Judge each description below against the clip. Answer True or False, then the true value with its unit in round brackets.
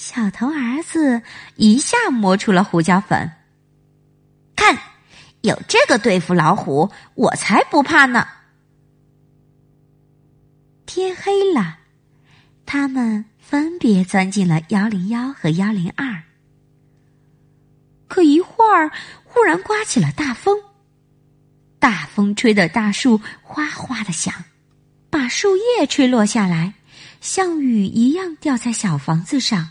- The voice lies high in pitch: True (195 Hz)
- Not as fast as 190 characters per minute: True (160 characters per minute)